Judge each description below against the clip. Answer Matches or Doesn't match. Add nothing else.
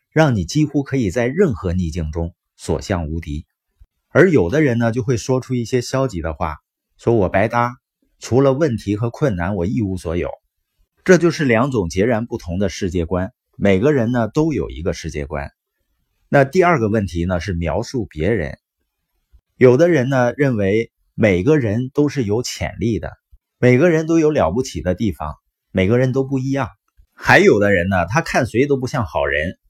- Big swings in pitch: Matches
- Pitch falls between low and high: Doesn't match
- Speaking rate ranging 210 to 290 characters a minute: Matches